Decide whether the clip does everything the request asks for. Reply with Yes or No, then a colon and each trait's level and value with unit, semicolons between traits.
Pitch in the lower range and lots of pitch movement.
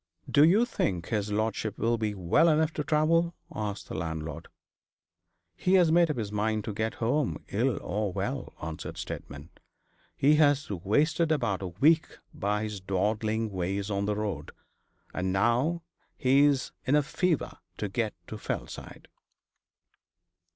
Yes: low, 110 Hz; wide, 6.9 semitones